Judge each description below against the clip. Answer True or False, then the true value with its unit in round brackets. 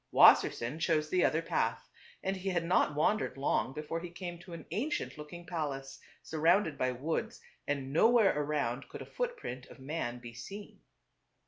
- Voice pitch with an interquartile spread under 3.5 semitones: False (4.8 semitones)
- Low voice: False (160 Hz)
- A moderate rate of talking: True (165 wpm)